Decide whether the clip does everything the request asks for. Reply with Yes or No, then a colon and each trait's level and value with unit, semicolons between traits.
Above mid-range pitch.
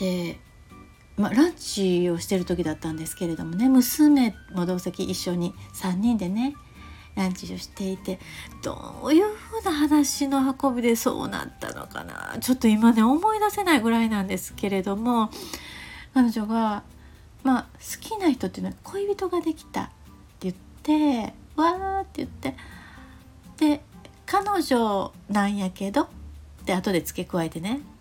Yes: high, 225 Hz